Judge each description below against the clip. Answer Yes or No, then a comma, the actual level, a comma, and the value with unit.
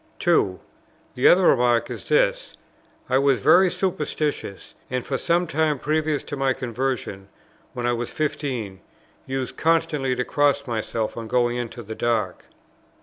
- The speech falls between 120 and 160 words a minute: Yes, average, 145 wpm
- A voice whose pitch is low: Yes, low, 130 Hz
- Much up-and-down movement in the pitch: No, average, 4.5 semitones